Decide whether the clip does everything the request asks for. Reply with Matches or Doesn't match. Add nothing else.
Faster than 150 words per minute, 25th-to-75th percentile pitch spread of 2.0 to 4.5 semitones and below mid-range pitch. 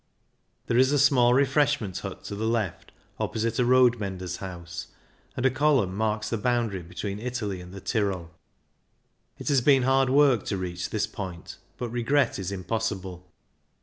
Doesn't match